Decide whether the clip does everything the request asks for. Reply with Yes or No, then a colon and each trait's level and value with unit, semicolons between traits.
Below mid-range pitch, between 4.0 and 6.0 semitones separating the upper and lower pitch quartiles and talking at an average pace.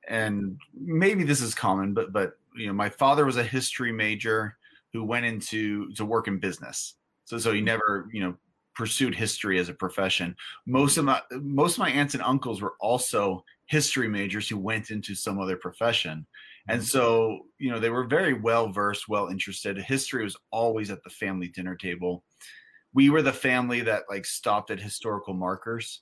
Yes: low, 110 Hz; average, 4.3 semitones; average, 185 wpm